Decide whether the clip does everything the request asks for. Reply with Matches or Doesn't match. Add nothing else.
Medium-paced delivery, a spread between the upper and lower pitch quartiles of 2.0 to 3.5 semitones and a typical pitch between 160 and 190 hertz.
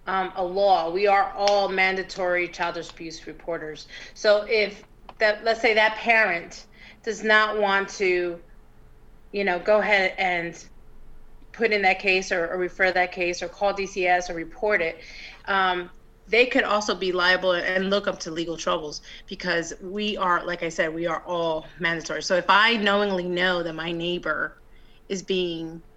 Matches